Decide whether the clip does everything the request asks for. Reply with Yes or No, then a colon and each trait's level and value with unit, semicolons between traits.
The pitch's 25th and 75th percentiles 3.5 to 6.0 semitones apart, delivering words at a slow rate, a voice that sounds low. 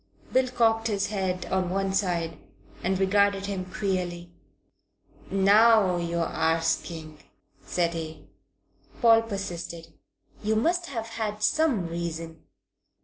No: average, 4.1 semitones; slow, 110 wpm; high, 190 Hz